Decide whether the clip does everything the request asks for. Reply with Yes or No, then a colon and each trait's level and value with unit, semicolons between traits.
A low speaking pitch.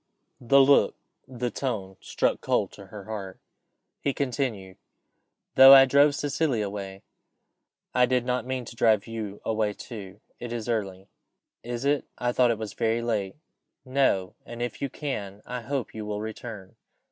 Yes: low, 115 Hz